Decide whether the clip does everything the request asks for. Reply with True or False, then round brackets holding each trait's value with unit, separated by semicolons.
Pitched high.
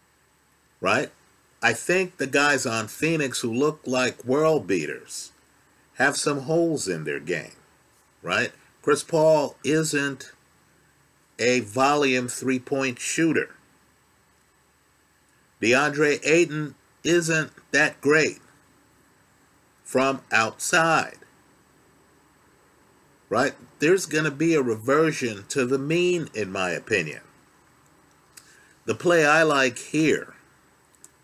False (140 Hz)